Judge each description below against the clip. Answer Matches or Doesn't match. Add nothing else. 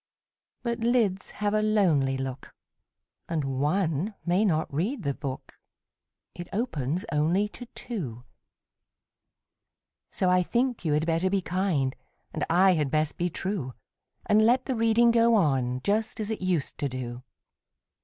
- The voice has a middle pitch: Matches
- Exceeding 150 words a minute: Doesn't match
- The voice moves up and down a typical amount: Doesn't match